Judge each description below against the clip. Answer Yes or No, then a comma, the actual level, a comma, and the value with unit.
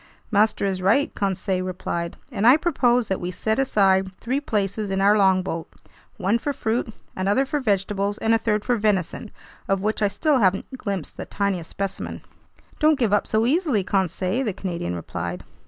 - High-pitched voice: Yes, high, 205 Hz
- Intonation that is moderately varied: Yes, average, 3.5 semitones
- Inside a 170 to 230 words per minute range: Yes, average, 175 wpm